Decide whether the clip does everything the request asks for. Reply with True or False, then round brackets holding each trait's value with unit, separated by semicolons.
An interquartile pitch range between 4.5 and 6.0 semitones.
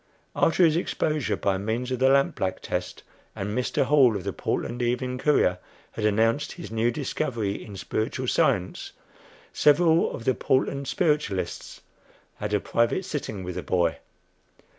True (5.4 semitones)